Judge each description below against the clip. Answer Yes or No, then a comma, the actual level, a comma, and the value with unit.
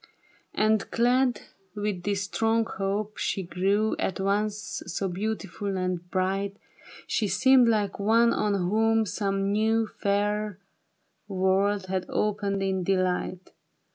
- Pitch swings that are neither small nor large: No, narrow, 2.0 semitones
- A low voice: No, high, 200 Hz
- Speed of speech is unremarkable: No, slow, 120 wpm